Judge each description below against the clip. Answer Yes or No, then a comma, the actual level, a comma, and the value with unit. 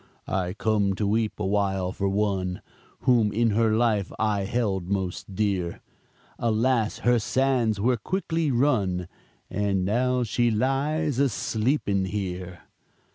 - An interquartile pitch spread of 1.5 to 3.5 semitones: No, average, 3.9 semitones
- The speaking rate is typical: No, slow, 130 wpm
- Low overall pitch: Yes, low, 105 Hz